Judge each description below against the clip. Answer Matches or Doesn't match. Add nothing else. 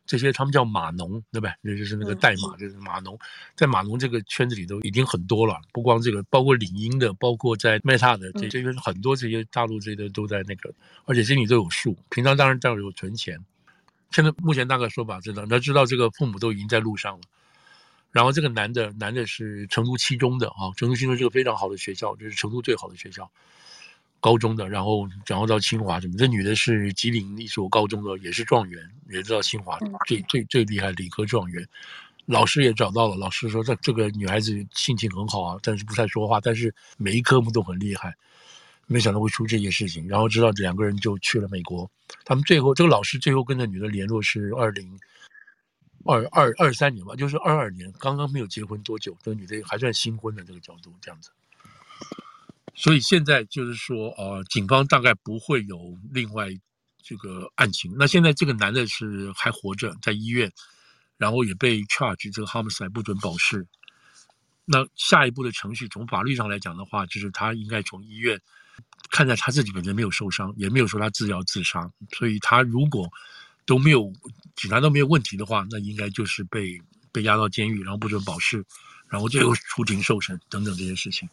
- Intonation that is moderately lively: Matches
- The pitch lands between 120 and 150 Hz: Doesn't match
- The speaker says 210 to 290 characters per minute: Doesn't match